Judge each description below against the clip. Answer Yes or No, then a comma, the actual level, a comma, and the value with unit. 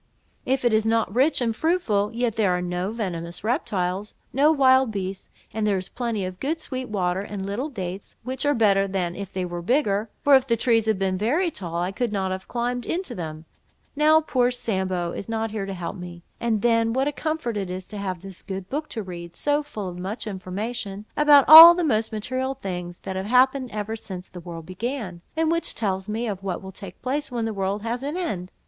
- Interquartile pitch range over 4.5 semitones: Yes, average, 5.2 semitones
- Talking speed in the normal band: No, fast, 220 wpm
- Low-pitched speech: No, high, 215 Hz